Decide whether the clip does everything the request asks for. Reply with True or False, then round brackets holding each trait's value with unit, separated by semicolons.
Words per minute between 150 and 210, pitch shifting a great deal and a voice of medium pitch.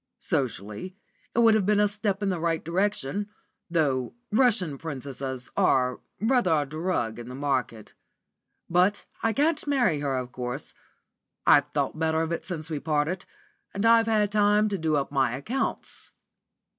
True (160 wpm; 7.2 semitones; 165 Hz)